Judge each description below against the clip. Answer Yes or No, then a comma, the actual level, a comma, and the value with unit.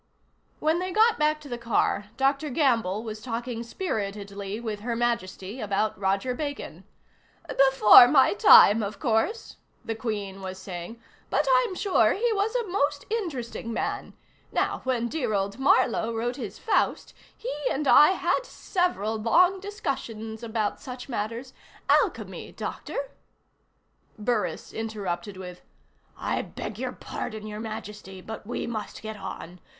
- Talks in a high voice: Yes, high, 230 Hz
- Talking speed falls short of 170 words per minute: Yes, average, 145 wpm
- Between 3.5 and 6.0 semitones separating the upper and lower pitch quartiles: Yes, average, 5.3 semitones